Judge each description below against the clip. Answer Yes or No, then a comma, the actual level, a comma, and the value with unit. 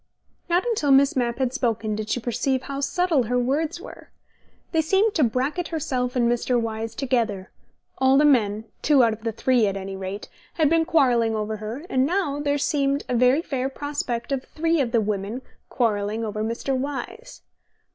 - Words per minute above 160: Yes, average, 185 wpm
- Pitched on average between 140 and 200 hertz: No, very high, 255 Hz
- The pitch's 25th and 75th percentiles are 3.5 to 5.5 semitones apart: Yes, average, 4.3 semitones